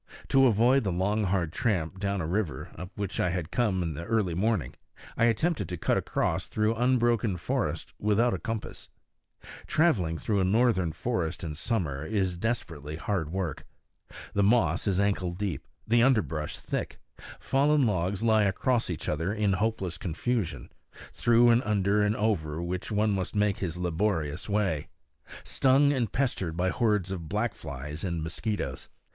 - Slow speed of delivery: No, average, 165 wpm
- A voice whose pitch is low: Yes, low, 100 Hz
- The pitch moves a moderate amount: Yes, average, 4.7 semitones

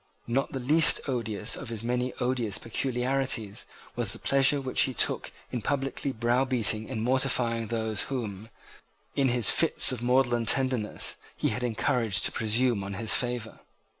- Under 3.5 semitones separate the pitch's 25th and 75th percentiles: Yes, average, 2.8 semitones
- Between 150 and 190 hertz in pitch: No, low, 120 Hz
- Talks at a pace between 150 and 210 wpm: Yes, average, 155 wpm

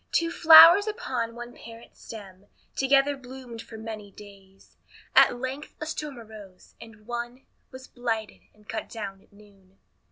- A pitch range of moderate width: Yes, average, 4.1 semitones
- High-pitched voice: Yes, high, 230 Hz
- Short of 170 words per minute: Yes, average, 150 wpm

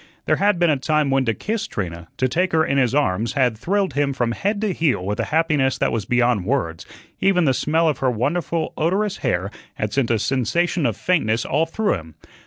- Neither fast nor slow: No, fast, 220 wpm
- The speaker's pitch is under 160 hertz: Yes, low, 135 Hz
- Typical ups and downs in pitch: No, wide, 6.4 semitones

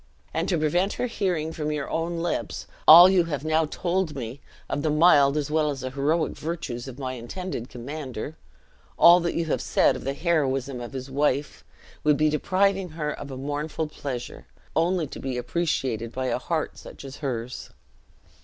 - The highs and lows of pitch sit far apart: No, average, 3.9 semitones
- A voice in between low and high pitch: Yes, medium, 150 Hz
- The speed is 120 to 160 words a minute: No, average, 180 wpm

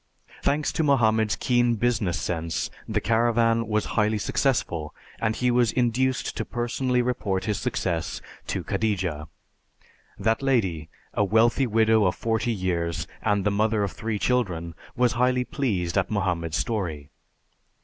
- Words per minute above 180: No, average, 140 wpm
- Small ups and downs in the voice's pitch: No, average, 4.5 semitones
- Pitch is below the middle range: Yes, low, 110 Hz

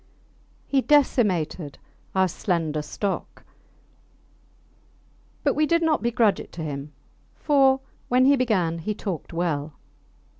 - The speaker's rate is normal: No, slow, 115 wpm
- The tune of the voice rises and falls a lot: Yes, wide, 8.5 semitones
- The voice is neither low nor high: No, high, 200 Hz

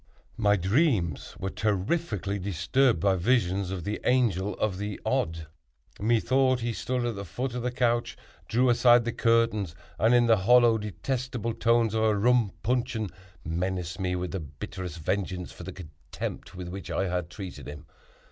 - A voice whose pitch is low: Yes, low, 105 Hz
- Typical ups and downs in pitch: Yes, average, 4.6 semitones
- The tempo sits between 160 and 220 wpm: Yes, average, 165 wpm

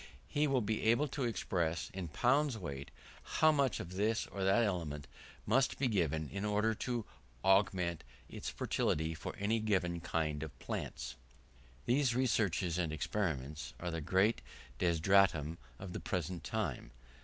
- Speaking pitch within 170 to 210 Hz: No, very low, 95 Hz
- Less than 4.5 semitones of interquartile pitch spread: No, wide, 5.4 semitones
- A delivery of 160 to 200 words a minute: No, average, 150 wpm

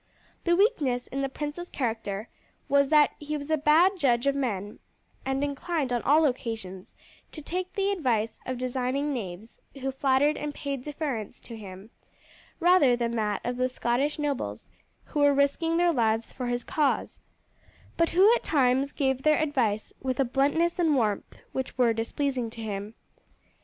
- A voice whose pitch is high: Yes, very high, 270 Hz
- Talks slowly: No, average, 170 wpm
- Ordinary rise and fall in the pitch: Yes, average, 4.0 semitones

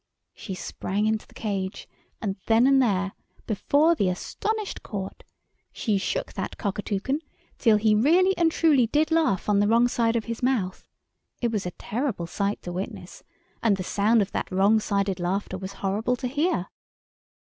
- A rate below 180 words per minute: Yes, average, 170 wpm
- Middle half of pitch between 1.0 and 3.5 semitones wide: No, average, 4.5 semitones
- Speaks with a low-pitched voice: No, high, 215 Hz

